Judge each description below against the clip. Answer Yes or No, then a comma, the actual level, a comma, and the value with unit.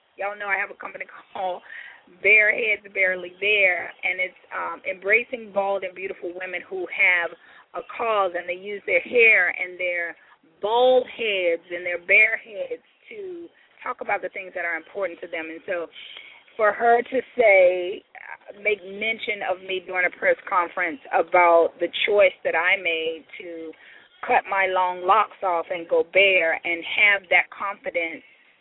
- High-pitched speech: Yes, high, 195 Hz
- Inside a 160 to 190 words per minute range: Yes, average, 165 wpm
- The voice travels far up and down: No, average, 3.5 semitones